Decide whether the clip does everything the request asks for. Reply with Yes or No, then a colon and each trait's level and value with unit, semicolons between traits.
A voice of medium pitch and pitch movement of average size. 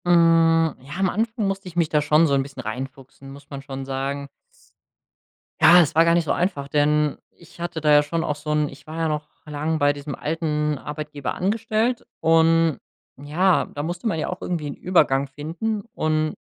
Yes: medium, 155 Hz; average, 3.0 semitones